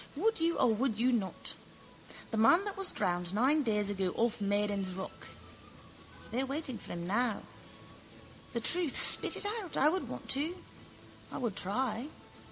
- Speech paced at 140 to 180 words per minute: Yes, average, 170 wpm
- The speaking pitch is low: No, high, 235 Hz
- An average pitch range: No, wide, 6.5 semitones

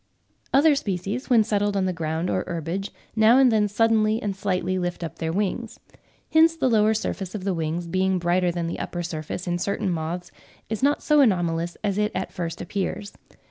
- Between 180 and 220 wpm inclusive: Yes, average, 195 wpm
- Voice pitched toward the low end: No, high, 190 Hz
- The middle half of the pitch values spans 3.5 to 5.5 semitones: Yes, average, 3.8 semitones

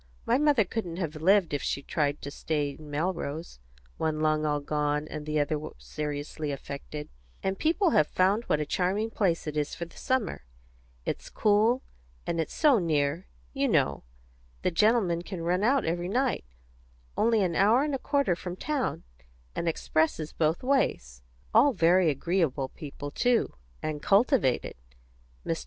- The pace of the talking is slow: No, average, 165 wpm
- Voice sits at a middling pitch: Yes, medium, 170 Hz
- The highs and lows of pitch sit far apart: Yes, wide, 6.1 semitones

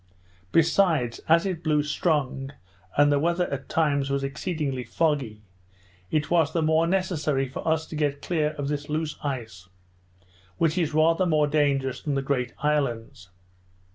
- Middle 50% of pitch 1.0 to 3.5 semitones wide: Yes, average, 2.8 semitones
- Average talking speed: Yes, average, 155 wpm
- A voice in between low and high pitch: Yes, medium, 150 Hz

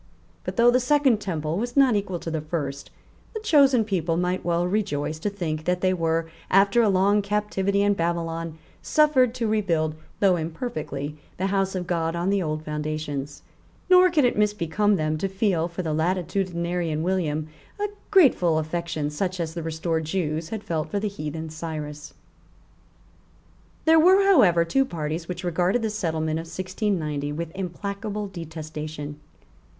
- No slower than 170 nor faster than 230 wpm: No, average, 160 wpm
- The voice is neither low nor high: Yes, medium, 175 Hz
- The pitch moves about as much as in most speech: Yes, average, 4.4 semitones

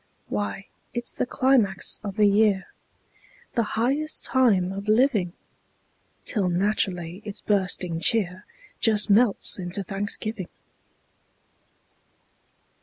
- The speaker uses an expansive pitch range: No, average, 3.2 semitones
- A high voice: Yes, high, 205 Hz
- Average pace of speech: No, slow, 100 wpm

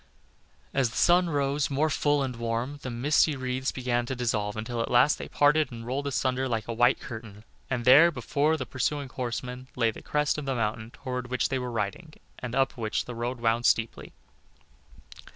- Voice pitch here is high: No, low, 125 Hz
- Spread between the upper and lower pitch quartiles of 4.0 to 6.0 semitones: No, average, 3.2 semitones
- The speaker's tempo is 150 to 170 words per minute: No, average, 195 wpm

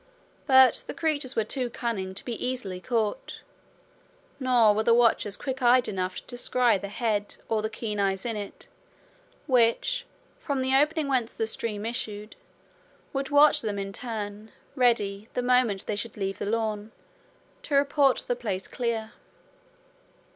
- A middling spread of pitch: Yes, average, 3.6 semitones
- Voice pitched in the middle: No, high, 230 Hz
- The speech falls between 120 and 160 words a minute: Yes, average, 155 wpm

